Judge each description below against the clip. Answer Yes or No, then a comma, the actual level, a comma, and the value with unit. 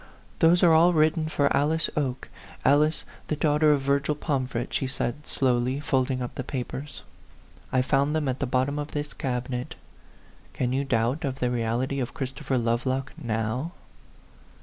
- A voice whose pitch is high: No, low, 135 Hz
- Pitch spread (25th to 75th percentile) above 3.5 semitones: No, average, 2.9 semitones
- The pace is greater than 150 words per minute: Yes, average, 165 wpm